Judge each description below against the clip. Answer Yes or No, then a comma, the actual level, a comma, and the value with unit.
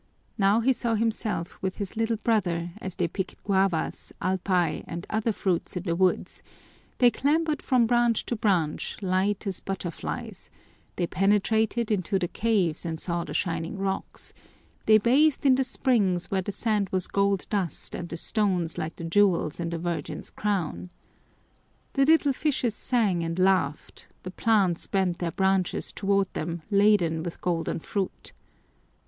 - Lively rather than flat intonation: No, average, 4.1 semitones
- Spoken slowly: No, average, 155 wpm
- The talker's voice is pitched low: No, high, 195 Hz